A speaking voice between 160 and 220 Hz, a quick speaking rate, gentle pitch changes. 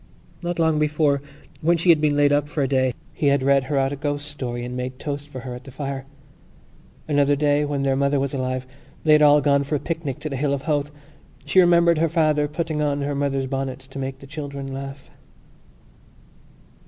No: medium, 145 Hz; fast, 215 wpm; narrow, 1.8 semitones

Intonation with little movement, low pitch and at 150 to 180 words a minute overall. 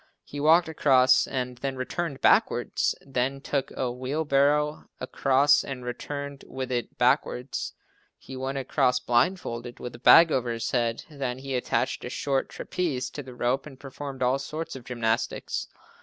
Yes: narrow, 2.2 semitones; low, 130 Hz; average, 160 wpm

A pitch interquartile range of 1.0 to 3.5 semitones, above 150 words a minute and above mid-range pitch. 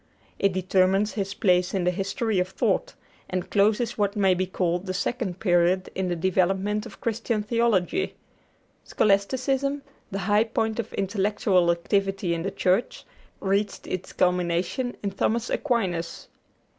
No: average, 2.9 semitones; average, 145 wpm; high, 195 Hz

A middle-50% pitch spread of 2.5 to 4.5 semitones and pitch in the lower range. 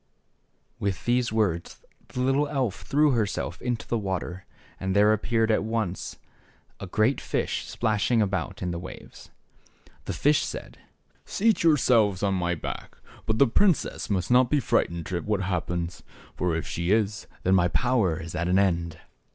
No: average, 5.0 semitones; low, 105 Hz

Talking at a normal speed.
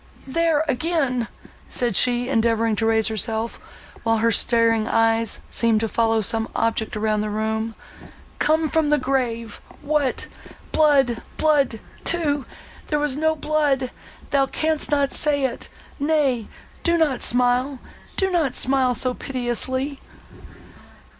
No: slow, 115 wpm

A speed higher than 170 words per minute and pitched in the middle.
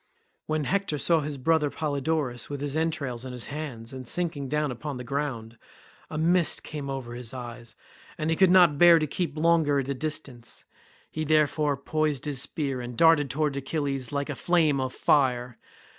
Yes: average, 185 wpm; medium, 145 Hz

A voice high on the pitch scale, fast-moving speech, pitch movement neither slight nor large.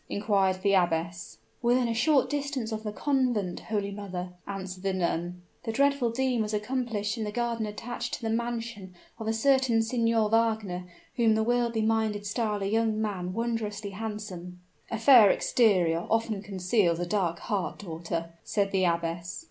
No: high, 215 Hz; average, 165 wpm; average, 3.6 semitones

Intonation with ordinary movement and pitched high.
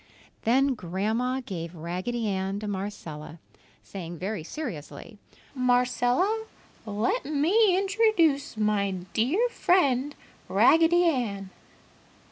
No: wide, 7.8 semitones; high, 240 Hz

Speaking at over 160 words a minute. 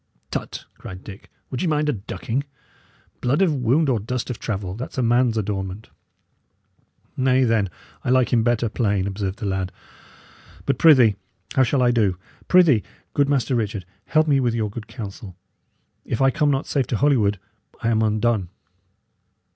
Yes: average, 170 wpm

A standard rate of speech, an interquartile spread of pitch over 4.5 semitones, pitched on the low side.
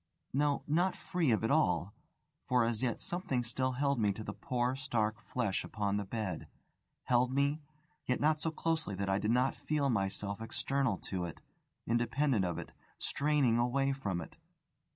Yes: average, 170 wpm; average, 4.9 semitones; low, 125 Hz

